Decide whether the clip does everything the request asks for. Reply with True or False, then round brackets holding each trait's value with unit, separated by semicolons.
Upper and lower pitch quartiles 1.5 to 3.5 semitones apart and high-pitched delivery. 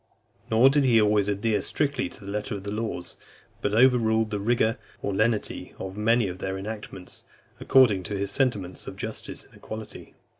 False (2.7 semitones; 105 Hz)